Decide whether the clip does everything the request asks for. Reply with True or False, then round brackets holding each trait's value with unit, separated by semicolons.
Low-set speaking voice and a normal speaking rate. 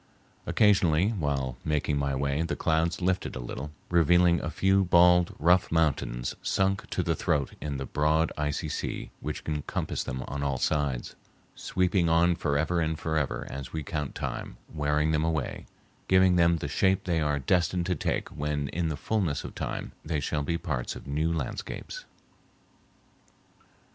True (80 Hz; 165 wpm)